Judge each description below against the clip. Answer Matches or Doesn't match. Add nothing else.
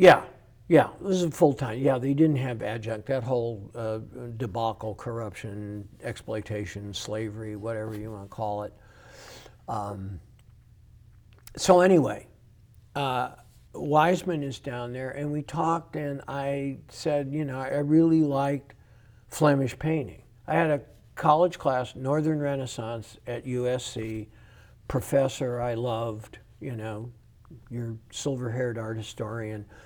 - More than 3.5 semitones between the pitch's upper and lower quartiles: Matches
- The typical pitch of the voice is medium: Doesn't match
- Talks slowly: Matches